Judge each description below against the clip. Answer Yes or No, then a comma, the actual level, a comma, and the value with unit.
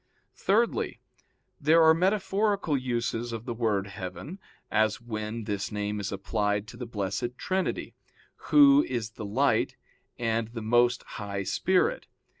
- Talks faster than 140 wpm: No, slow, 135 wpm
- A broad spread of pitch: Yes, wide, 7.1 semitones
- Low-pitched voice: Yes, low, 115 Hz